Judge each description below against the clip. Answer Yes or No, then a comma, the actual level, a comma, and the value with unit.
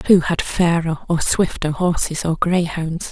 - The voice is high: No, medium, 170 Hz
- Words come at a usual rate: Yes, average, 155 wpm